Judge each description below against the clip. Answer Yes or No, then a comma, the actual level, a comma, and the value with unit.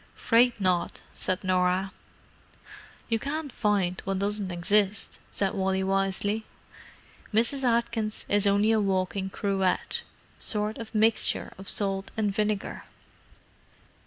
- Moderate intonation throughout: No, narrow, 2.3 semitones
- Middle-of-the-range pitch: No, high, 205 Hz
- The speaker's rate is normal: No, slow, 110 wpm